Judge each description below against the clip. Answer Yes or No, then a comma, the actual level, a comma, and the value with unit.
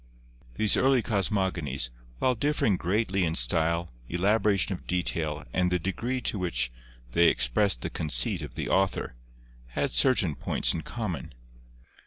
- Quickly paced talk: No, average, 140 wpm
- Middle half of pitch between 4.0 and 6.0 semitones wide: Yes, average, 4.9 semitones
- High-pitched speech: No, very low, 90 Hz